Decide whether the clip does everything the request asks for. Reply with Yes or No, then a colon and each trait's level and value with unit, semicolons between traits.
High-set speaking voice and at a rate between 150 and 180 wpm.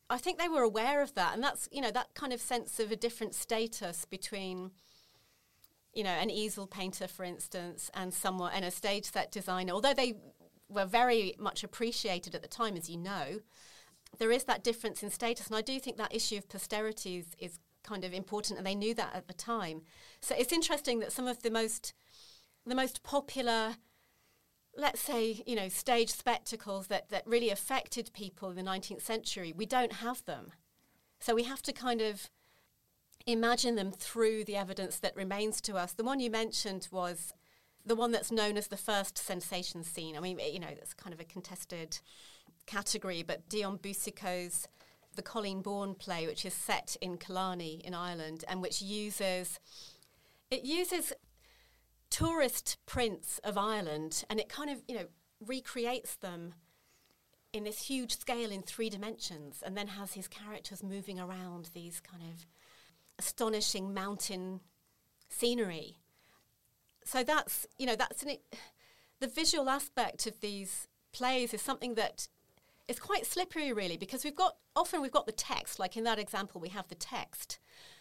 Yes: high, 210 Hz; average, 175 wpm